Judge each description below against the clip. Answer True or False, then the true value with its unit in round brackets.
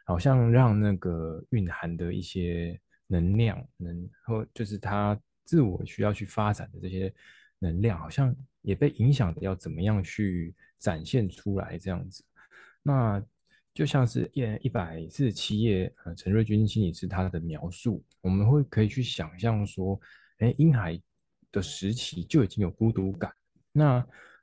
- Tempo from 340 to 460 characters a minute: False (230 characters per minute)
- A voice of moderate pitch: False (105 Hz)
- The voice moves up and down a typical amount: True (4.5 semitones)